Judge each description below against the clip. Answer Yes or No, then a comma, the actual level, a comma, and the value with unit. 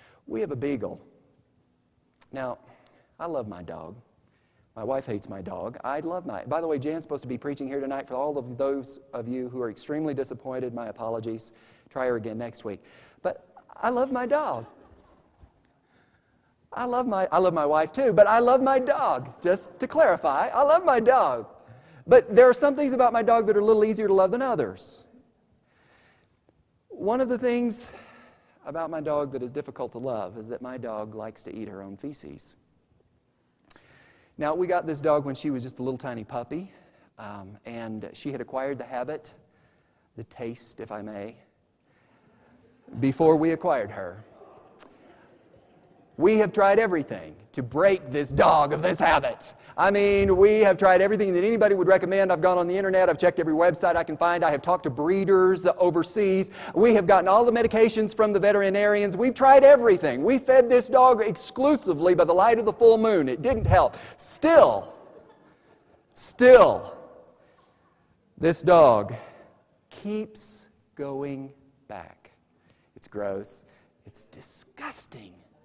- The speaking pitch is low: No, medium, 175 Hz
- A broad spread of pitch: Yes, wide, 8.6 semitones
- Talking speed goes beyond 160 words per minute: Yes, average, 170 wpm